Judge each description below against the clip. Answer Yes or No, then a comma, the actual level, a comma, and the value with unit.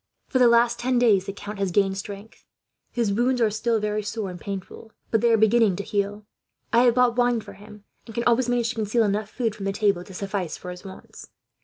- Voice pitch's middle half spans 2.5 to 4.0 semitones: Yes, average, 2.9 semitones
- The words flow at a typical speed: No, fast, 235 wpm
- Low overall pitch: No, high, 215 Hz